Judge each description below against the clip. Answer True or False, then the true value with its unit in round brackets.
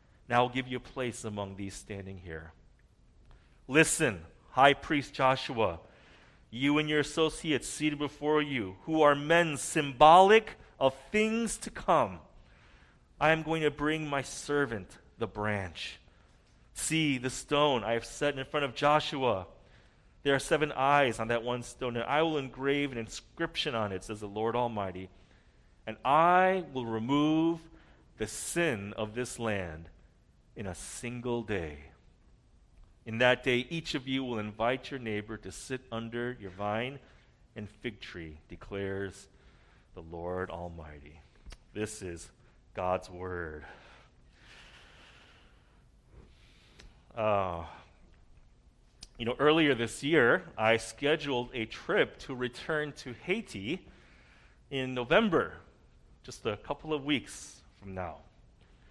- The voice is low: True (120 Hz)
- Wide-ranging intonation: True (7.0 semitones)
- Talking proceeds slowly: True (130 wpm)